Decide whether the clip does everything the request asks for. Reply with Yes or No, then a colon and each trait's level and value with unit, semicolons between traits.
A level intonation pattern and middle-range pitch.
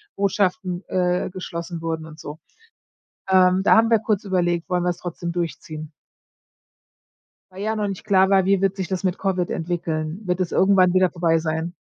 Yes: narrow, 2.2 semitones; medium, 180 Hz